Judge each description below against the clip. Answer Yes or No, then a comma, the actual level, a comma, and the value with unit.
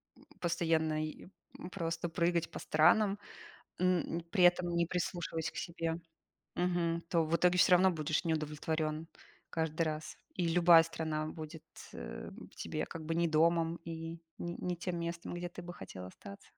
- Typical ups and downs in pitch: No, narrow, 1.6 semitones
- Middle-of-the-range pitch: Yes, medium, 165 Hz